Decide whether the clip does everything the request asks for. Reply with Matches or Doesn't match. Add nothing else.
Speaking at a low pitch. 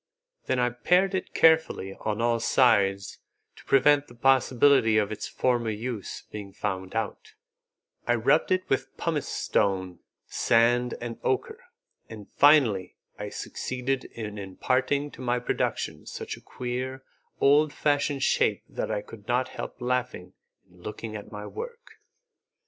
Matches